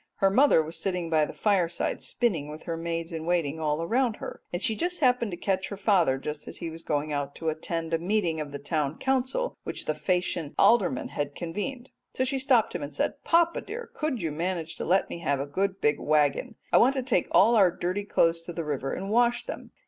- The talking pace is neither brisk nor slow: No, fast, 230 wpm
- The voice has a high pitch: No, medium, 175 Hz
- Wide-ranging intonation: Yes, wide, 6.5 semitones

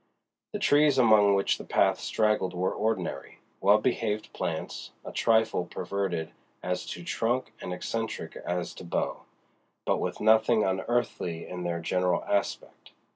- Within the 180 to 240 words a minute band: No, average, 140 wpm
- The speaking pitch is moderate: No, low, 100 Hz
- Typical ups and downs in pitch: Yes, average, 3.8 semitones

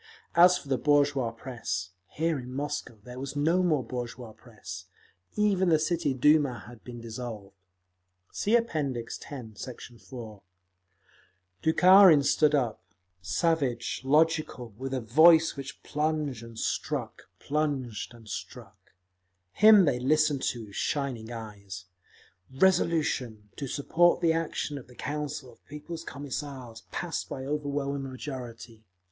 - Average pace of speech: No, slow, 130 wpm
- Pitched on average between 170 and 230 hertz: No, low, 135 Hz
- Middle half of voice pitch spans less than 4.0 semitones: No, average, 4.5 semitones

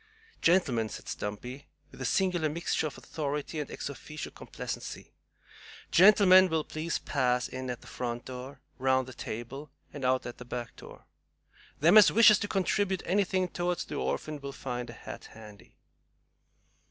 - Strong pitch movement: Yes, wide, 6.0 semitones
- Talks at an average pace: Yes, average, 160 wpm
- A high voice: No, medium, 145 Hz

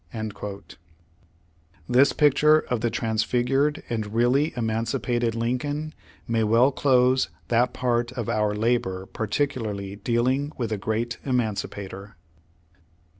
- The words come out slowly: Yes, slow, 110 wpm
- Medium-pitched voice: No, low, 120 Hz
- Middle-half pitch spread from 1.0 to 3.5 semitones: Yes, average, 2.8 semitones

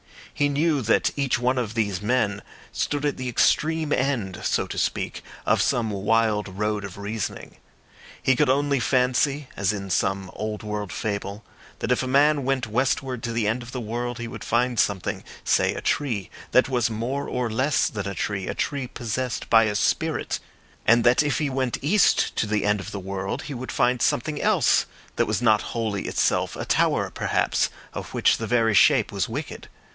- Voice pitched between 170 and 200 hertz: No, low, 115 Hz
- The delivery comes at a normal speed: Yes, average, 190 wpm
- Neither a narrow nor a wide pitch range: Yes, average, 3.9 semitones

